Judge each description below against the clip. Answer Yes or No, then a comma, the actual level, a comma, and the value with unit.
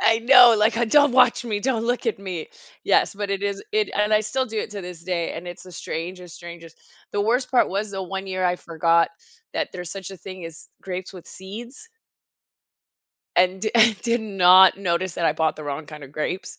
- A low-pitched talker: No, high, 190 Hz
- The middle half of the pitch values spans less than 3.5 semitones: No, average, 4.2 semitones